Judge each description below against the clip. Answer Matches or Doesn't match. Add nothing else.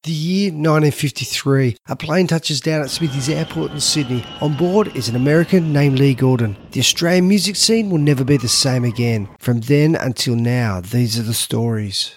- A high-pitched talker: Doesn't match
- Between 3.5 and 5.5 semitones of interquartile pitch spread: Matches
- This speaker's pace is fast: Doesn't match